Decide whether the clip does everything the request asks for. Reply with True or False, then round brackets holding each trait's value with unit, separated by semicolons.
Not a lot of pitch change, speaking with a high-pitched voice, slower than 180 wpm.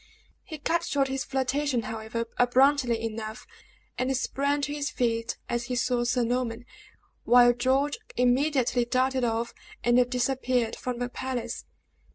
True (1.9 semitones; 250 Hz; 140 wpm)